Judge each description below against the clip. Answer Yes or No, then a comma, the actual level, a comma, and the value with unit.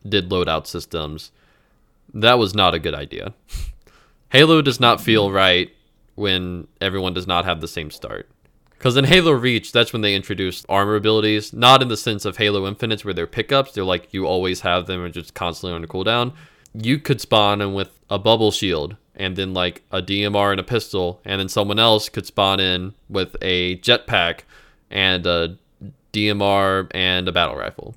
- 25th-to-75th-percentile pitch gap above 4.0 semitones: No, average, 3.3 semitones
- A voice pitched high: No, low, 100 Hz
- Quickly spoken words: No, average, 185 wpm